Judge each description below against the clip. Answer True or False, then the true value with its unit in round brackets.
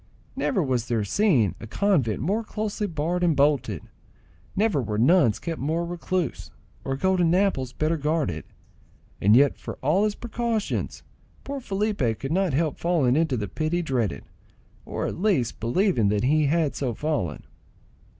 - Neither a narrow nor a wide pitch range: False (6.9 semitones)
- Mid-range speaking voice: True (155 Hz)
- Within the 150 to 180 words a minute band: True (155 wpm)